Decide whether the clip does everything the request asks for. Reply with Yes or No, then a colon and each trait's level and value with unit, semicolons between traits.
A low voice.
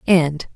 No: medium, 165 Hz